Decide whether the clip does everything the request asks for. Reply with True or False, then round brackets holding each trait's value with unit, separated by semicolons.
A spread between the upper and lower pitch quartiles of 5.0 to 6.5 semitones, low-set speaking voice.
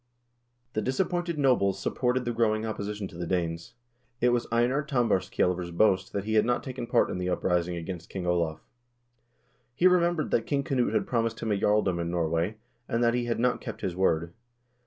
True (5.6 semitones; 110 Hz)